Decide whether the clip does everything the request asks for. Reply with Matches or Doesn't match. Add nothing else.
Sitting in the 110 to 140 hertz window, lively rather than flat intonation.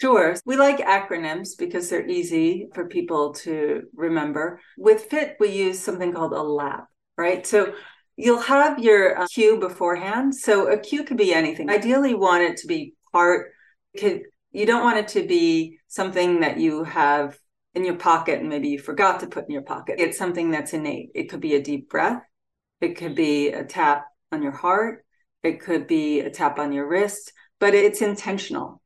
Doesn't match